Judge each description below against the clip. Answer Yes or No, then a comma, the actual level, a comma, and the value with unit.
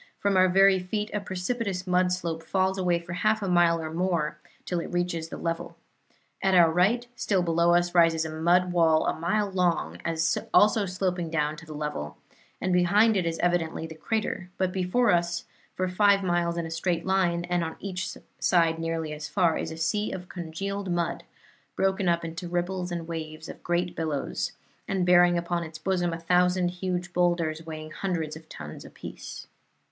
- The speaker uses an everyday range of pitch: No, narrow, 2.2 semitones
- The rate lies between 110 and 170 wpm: No, average, 185 wpm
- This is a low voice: No, medium, 175 Hz